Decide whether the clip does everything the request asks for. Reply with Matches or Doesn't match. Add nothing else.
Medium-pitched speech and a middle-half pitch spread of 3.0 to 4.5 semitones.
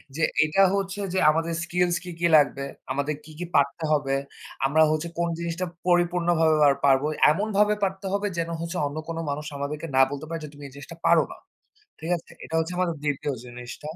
Matches